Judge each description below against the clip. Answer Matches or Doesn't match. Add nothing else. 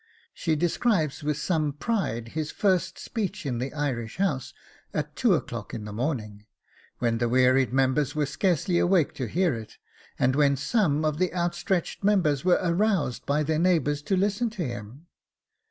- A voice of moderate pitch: Matches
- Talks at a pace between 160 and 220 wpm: Matches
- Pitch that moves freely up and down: Matches